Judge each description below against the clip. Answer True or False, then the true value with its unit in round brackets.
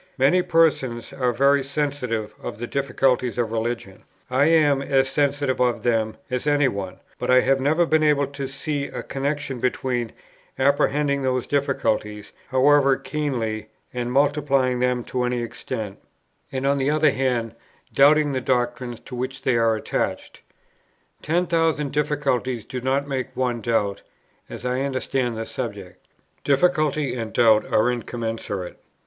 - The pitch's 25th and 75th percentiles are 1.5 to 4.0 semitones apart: True (2.9 semitones)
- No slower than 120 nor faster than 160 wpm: True (150 wpm)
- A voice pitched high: False (130 Hz)